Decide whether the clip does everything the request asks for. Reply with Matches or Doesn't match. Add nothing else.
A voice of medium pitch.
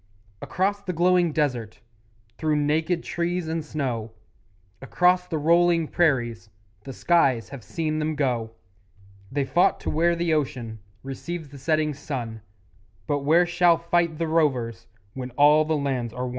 Matches